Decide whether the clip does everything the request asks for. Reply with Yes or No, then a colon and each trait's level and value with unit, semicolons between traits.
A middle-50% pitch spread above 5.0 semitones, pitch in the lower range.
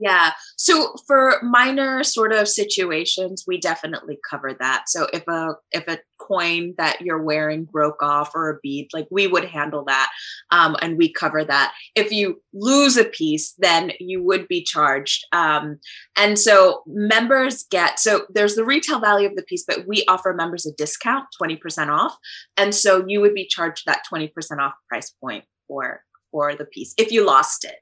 No: wide, 5.5 semitones; medium, 185 Hz